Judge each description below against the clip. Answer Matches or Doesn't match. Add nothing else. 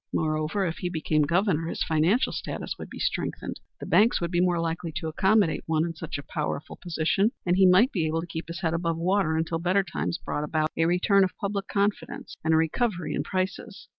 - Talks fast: Matches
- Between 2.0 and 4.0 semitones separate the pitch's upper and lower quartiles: Matches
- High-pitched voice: Doesn't match